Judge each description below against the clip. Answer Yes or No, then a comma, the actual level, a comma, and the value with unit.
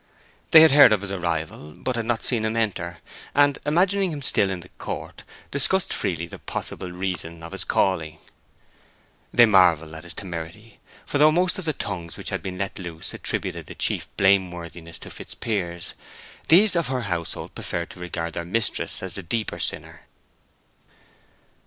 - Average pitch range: No, wide, 6.3 semitones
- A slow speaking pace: No, average, 175 wpm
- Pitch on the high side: No, very low, 95 Hz